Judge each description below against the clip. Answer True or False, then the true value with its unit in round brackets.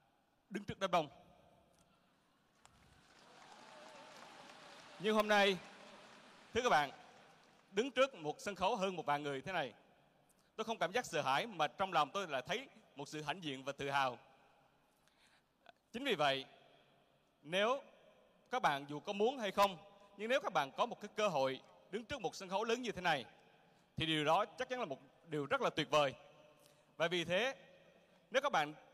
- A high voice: False (180 Hz)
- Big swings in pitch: True (5.8 semitones)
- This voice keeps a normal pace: True (180 wpm)